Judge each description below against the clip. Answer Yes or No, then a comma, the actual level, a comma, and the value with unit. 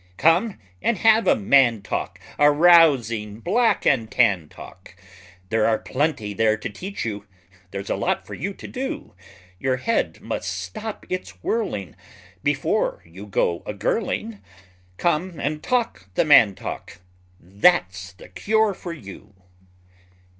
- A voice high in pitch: No, low, 135 Hz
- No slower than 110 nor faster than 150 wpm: Yes, average, 140 wpm